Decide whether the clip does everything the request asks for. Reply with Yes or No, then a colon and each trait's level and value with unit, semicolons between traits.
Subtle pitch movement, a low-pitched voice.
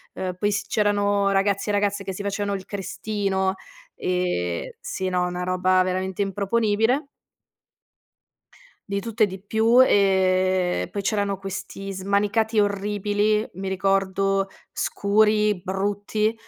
No: narrow, 1.5 semitones; high, 200 Hz